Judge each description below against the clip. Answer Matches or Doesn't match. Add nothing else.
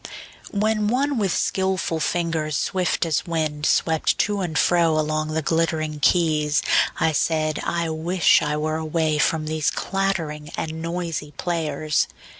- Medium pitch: Matches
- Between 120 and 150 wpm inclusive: Matches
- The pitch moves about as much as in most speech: Doesn't match